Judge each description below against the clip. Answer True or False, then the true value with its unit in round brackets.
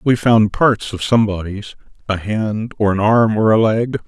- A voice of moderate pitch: False (110 Hz)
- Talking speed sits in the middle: True (190 wpm)